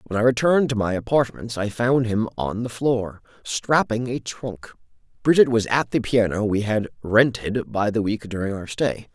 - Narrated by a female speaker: No, male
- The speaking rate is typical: Yes, average, 190 wpm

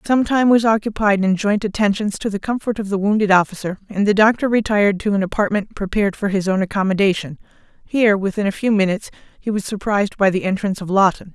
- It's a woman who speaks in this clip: Yes, female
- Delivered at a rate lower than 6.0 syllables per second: No, 6.4 syllables/s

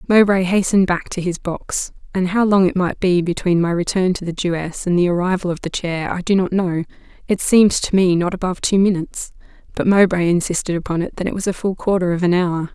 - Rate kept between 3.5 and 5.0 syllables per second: No, 5.9 syllables/s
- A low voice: No, medium, 180 Hz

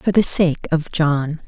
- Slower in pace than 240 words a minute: Yes, fast, 205 wpm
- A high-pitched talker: No, medium, 160 Hz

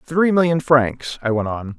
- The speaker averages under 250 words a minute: Yes, average, 200 wpm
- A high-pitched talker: No, low, 135 Hz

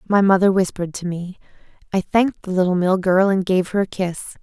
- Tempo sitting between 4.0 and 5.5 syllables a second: No, 5.9 syllables/s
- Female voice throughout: Yes, female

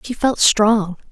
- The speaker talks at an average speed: Yes, average, 160 wpm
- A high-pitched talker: Yes, high, 215 Hz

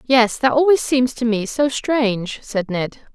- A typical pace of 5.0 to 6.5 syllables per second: No, 4.2 syllables/s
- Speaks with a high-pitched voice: Yes, high, 240 Hz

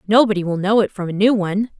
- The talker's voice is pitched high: Yes, high, 200 Hz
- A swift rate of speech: Yes, fast, 265 wpm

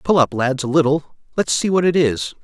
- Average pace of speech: No, fast, 245 wpm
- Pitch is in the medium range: Yes, medium, 150 Hz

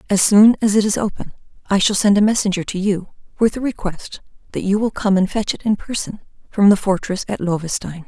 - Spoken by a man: No, female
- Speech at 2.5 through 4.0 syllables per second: No, 5.7 syllables/s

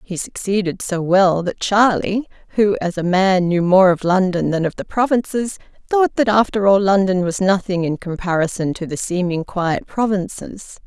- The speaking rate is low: No, average, 175 wpm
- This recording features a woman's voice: Yes, female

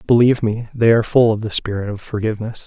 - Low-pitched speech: Yes, low, 110 Hz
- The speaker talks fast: Yes, fast, 225 wpm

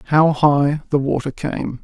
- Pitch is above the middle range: No, medium, 145 Hz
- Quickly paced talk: No, average, 165 wpm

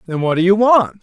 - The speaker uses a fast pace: Yes, fast, 295 wpm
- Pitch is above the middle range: Yes, high, 195 Hz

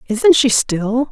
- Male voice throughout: No, female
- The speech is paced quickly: No, average, 160 wpm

